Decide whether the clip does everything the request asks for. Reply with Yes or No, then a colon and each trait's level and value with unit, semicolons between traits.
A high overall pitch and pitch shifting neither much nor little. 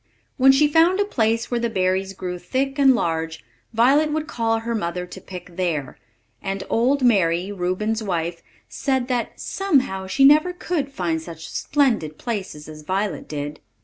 No: high, 215 Hz; wide, 7.1 semitones